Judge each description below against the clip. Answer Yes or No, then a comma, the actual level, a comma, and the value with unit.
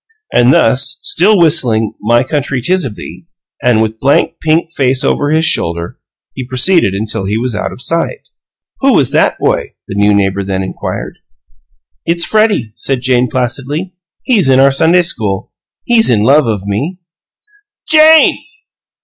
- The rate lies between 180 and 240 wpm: No, average, 160 wpm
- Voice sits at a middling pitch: No, low, 130 Hz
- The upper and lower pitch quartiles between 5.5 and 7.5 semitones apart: Yes, wide, 7.1 semitones